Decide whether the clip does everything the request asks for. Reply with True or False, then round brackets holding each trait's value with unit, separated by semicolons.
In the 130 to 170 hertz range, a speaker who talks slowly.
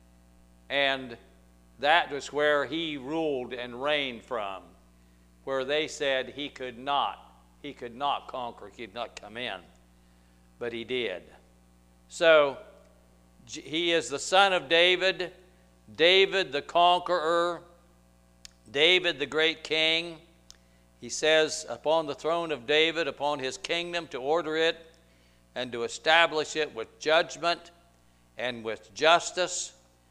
True (135 Hz; 125 wpm)